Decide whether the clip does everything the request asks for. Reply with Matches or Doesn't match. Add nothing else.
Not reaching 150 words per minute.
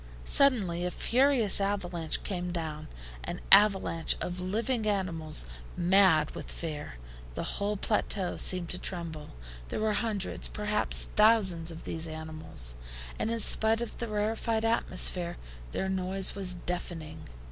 Matches